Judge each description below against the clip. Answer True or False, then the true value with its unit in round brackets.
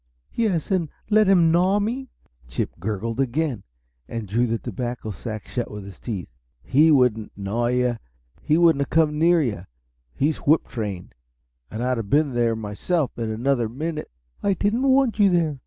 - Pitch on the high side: False (130 Hz)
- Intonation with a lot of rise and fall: True (6.8 semitones)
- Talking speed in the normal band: True (170 wpm)